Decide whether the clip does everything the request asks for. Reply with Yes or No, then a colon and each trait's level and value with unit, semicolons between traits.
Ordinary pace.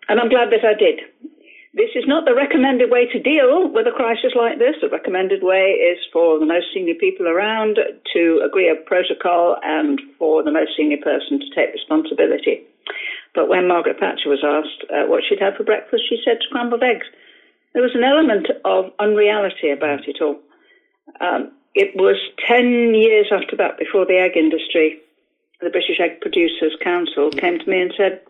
Yes: average, 185 wpm